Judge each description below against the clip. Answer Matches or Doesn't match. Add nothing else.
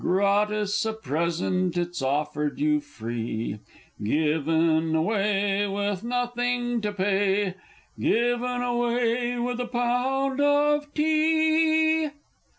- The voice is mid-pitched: Doesn't match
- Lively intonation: Matches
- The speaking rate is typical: Doesn't match